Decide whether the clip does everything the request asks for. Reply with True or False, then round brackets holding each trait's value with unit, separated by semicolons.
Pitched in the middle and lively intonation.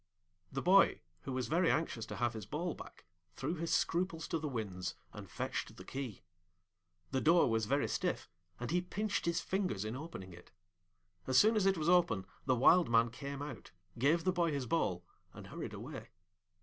True (145 Hz; 6.6 semitones)